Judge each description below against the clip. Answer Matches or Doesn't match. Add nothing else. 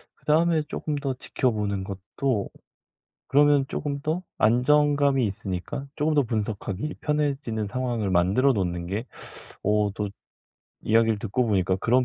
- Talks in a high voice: Doesn't match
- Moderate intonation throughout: Doesn't match